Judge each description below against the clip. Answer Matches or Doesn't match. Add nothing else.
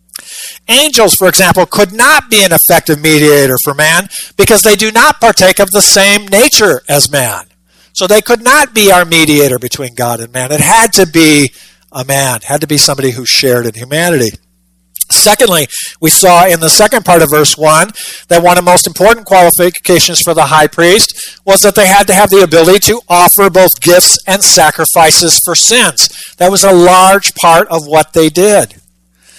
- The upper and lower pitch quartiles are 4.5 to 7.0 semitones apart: Matches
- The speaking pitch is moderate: Matches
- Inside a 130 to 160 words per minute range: Doesn't match